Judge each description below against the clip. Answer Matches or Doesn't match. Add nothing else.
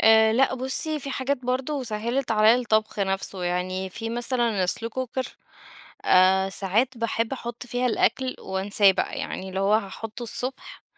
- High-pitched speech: Matches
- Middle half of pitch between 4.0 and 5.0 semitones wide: Matches